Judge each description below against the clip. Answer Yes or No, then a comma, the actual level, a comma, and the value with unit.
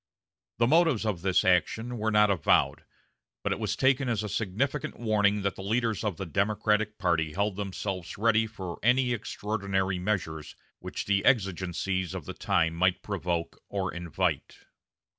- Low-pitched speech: Yes, low, 100 Hz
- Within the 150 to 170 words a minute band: Yes, average, 160 wpm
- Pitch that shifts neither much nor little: Yes, average, 3.1 semitones